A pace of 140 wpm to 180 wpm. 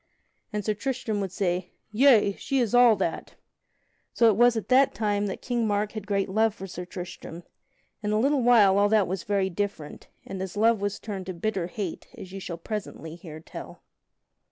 No: average, 200 wpm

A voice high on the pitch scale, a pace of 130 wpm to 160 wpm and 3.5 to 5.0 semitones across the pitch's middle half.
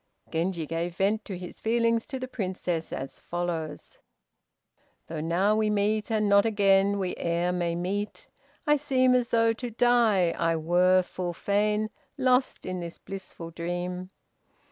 Yes: high, 195 Hz; average, 150 wpm; average, 3.9 semitones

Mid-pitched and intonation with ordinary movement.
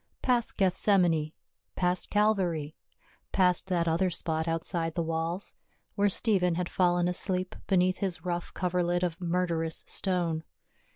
No: medium, 180 Hz; narrow, 2.0 semitones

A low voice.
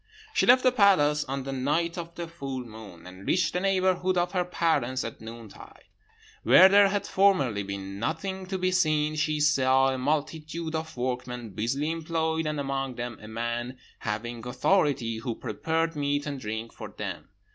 No: medium, 145 Hz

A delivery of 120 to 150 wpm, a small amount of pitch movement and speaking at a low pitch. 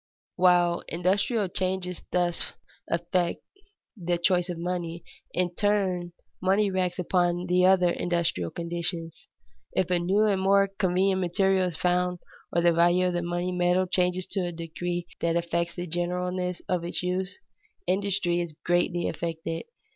No: average, 145 wpm; narrow, 1.2 semitones; medium, 180 Hz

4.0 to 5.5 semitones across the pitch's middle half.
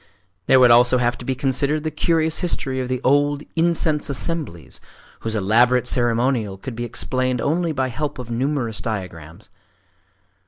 No: average, 3.6 semitones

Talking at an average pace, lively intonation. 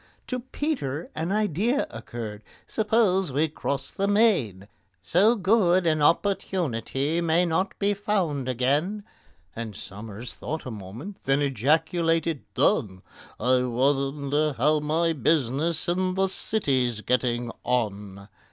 No: slow, 120 wpm; wide, 7.0 semitones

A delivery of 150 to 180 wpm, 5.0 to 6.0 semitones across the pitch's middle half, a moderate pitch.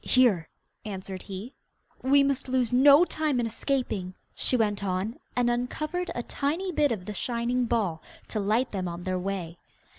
No: average, 170 wpm; average, 5.3 semitones; high, 235 Hz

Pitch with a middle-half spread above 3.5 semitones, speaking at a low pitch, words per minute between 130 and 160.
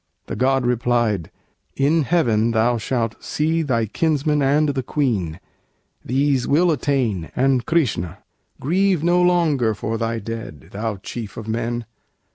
Yes: average, 4.7 semitones; low, 125 Hz; slow, 135 wpm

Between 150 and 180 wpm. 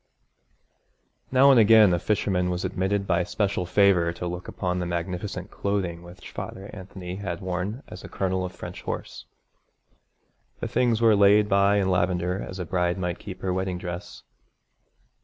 Yes: average, 165 wpm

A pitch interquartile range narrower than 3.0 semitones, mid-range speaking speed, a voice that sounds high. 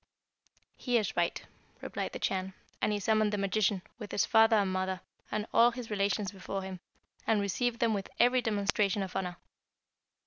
Yes: narrow, 2.6 semitones; average, 175 wpm; high, 205 Hz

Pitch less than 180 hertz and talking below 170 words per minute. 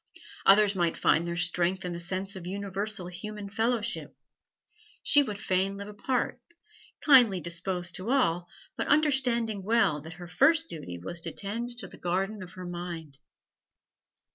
No: high, 195 Hz; average, 150 wpm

